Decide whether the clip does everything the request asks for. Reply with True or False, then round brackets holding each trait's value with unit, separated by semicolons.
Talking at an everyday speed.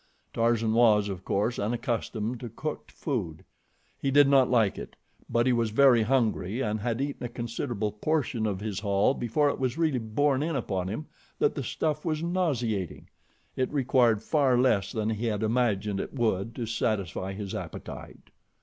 True (175 wpm)